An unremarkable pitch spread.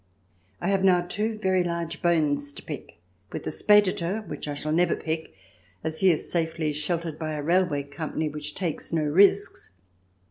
Yes: average, 3.3 semitones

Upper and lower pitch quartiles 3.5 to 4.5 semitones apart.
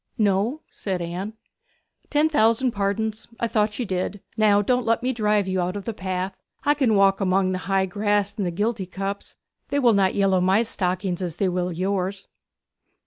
No: average, 2.7 semitones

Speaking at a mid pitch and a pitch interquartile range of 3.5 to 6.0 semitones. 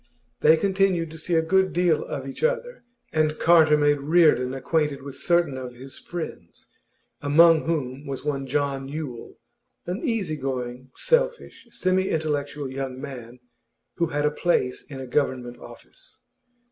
Yes: medium, 150 Hz; average, 4.2 semitones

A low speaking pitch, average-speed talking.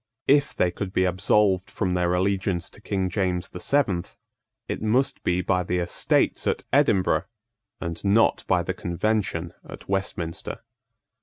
Yes: very low, 95 Hz; average, 150 wpm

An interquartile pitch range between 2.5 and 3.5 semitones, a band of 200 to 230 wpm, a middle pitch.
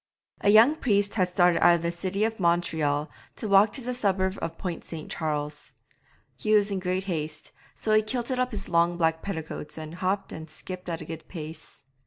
No: average, 4.0 semitones; fast, 205 wpm; medium, 180 Hz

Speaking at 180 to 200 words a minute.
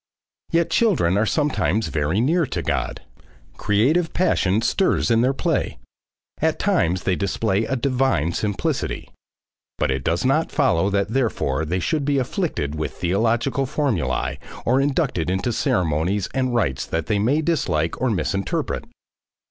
No: average, 145 wpm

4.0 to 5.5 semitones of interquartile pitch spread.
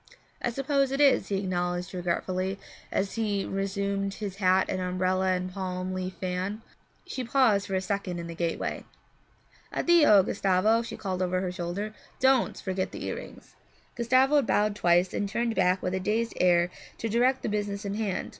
No: average, 3.3 semitones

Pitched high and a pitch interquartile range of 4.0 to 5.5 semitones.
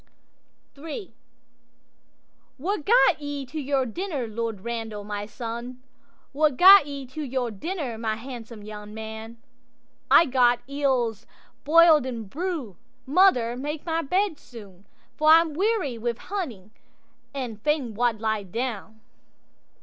Yes: very high, 255 Hz; average, 5.1 semitones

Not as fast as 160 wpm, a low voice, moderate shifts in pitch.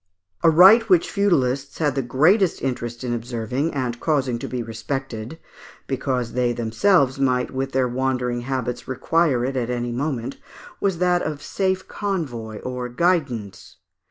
Yes: average, 150 wpm; low, 130 Hz; average, 4.6 semitones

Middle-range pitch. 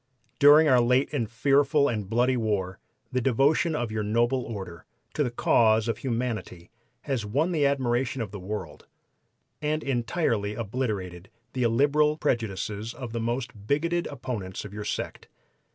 No: low, 120 Hz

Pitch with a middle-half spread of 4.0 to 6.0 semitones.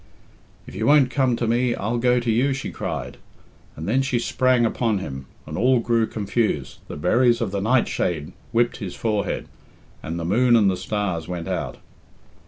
Yes: average, 4.9 semitones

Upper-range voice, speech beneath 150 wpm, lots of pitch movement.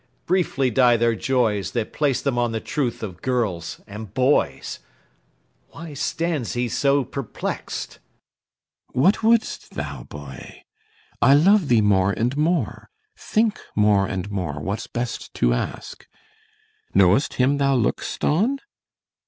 No: low, 120 Hz; slow, 135 wpm; wide, 6.0 semitones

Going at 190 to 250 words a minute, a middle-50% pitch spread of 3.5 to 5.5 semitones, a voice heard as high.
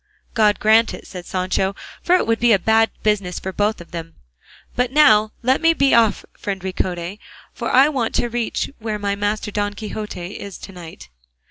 No: average, 195 wpm; average, 3.1 semitones; high, 210 Hz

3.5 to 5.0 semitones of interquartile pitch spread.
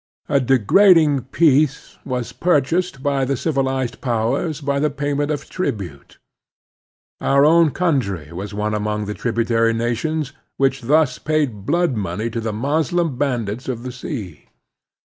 Yes: average, 4.6 semitones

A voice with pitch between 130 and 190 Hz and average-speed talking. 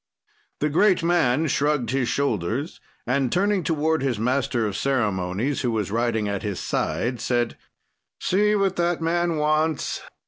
Yes: medium, 140 Hz; average, 145 wpm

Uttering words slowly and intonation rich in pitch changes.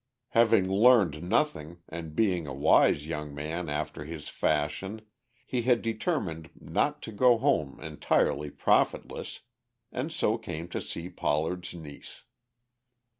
Yes: slow, 125 wpm; wide, 6.7 semitones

